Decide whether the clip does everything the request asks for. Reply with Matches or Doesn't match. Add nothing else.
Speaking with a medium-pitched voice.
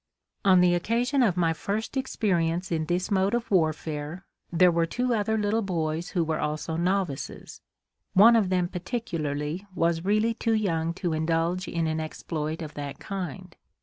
Matches